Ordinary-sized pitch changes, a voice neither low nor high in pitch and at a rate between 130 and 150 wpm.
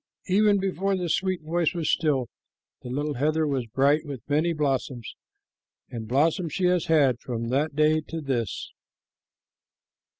Yes: average, 4.3 semitones; medium, 150 Hz; average, 145 wpm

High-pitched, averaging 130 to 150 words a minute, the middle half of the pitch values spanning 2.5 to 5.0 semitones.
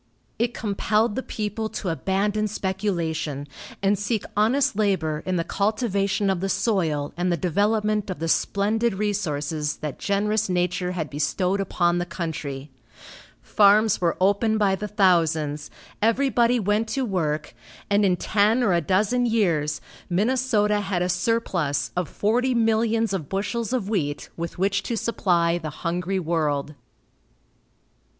Yes: high, 195 Hz; average, 145 wpm; average, 4.0 semitones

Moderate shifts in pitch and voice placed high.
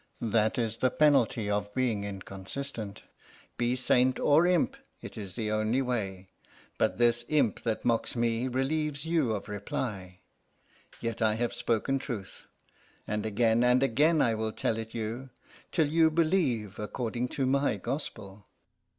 No: average, 3.9 semitones; low, 120 Hz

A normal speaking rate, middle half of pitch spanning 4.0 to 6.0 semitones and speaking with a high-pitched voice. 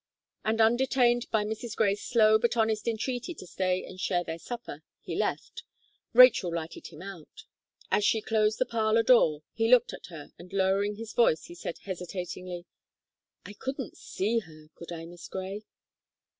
Yes: average, 170 wpm; average, 4.3 semitones; high, 210 Hz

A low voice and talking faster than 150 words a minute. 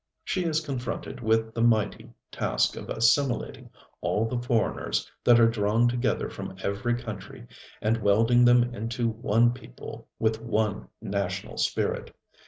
No: low, 115 Hz; average, 140 wpm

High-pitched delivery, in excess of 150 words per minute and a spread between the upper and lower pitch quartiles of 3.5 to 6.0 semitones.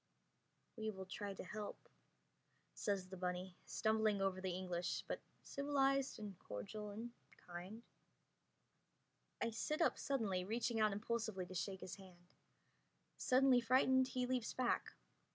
No: high, 210 Hz; slow, 135 wpm; average, 4.5 semitones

